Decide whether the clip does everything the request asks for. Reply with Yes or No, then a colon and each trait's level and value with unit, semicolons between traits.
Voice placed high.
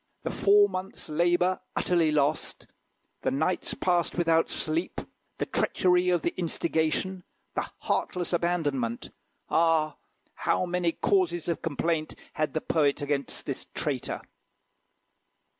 No: medium, 170 Hz